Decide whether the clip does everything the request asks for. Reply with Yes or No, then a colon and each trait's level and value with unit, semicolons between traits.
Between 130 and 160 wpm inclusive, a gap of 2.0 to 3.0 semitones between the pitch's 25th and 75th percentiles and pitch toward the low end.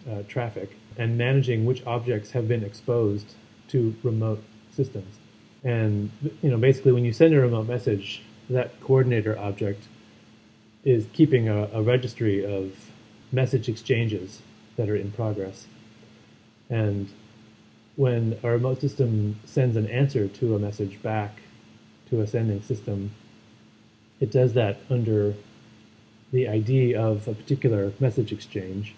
Yes: slow, 135 wpm; average, 2.7 semitones; low, 110 Hz